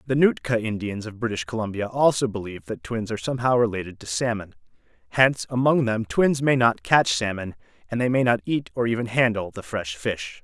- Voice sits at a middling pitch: No, low, 115 Hz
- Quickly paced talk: No, average, 195 wpm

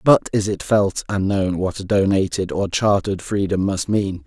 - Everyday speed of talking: Yes, average, 195 wpm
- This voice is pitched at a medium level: No, very low, 95 Hz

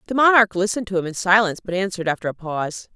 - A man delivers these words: No, female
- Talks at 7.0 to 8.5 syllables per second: Yes, 7.8 syllables/s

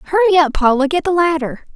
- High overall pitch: Yes, very high, 315 Hz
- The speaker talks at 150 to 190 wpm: No, fast, 205 wpm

